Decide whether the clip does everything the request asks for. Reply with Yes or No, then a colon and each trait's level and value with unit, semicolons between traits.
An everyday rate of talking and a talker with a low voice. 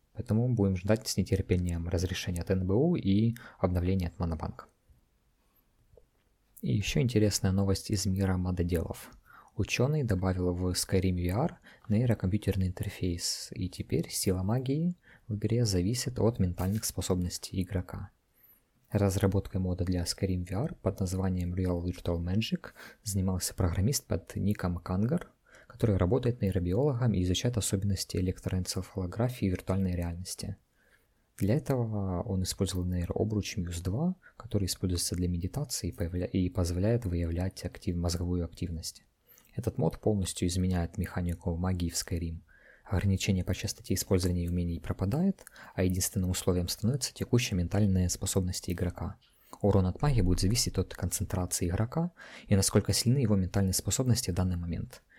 Yes: average, 130 wpm; very low, 95 Hz